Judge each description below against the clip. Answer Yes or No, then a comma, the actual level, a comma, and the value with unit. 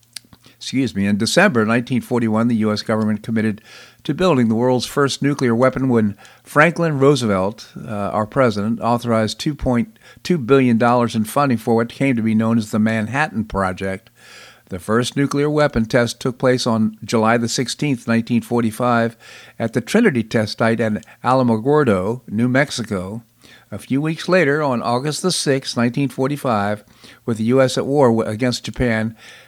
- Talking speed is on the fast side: No, average, 145 wpm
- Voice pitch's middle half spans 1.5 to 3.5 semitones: Yes, average, 3.1 semitones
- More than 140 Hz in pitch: No, low, 120 Hz